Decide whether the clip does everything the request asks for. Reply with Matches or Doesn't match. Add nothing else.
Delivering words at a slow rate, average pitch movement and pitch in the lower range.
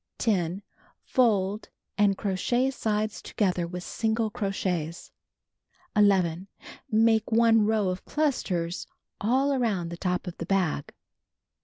Doesn't match